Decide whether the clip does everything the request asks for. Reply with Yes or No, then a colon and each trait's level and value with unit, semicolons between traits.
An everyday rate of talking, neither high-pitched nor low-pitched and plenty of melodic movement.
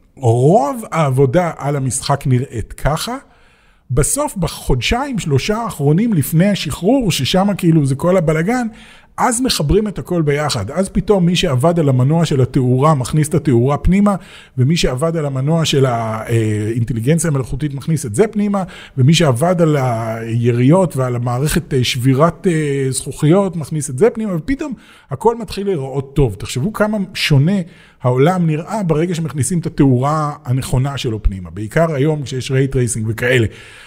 Yes: average, 140 wpm; medium, 155 Hz; wide, 5.8 semitones